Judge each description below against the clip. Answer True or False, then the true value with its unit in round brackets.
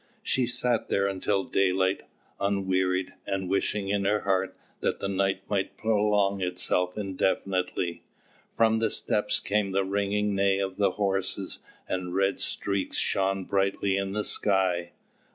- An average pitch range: False (1.3 semitones)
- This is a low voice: True (95 Hz)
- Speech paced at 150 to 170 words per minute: False (140 wpm)